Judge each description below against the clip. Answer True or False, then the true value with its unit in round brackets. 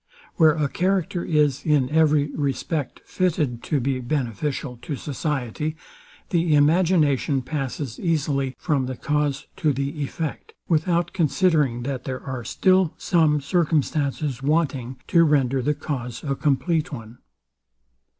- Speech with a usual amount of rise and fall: True (3.0 semitones)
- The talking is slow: True (125 wpm)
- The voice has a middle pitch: True (145 Hz)